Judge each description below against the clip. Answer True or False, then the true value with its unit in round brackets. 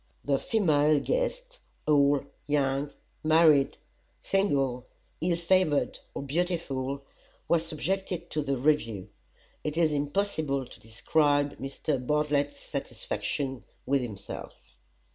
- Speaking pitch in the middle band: True (145 Hz)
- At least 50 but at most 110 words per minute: True (105 wpm)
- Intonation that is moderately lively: True (3.4 semitones)